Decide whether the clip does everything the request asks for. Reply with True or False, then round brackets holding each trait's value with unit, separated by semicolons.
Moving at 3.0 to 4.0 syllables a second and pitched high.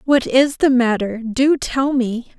True (3.7 syllables/s; 250 Hz)